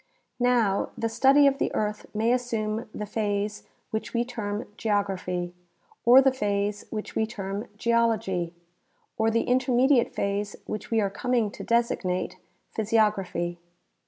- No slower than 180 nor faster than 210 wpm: No, average, 145 wpm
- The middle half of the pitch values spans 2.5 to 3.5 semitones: Yes, average, 2.8 semitones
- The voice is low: No, high, 215 Hz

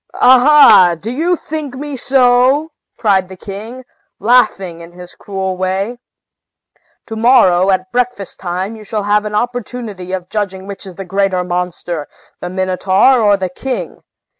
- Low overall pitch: No, high, 200 Hz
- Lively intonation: No, average, 4.8 semitones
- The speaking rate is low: No, average, 150 wpm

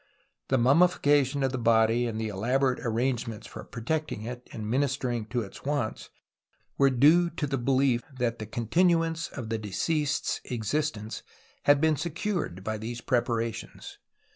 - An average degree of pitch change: Yes, average, 4.2 semitones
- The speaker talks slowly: No, average, 160 wpm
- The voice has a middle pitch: No, low, 125 Hz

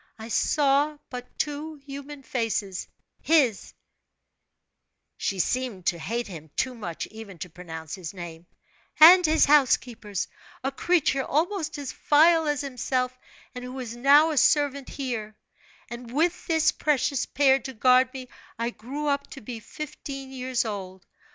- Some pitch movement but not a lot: Yes, average, 4.7 semitones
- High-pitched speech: Yes, very high, 260 Hz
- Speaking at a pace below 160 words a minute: Yes, average, 145 wpm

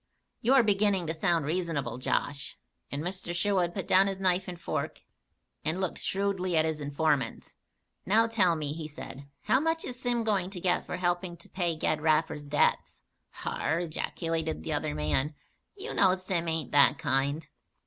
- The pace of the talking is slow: No, average, 175 wpm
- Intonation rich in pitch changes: No, average, 3.9 semitones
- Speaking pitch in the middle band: Yes, medium, 175 Hz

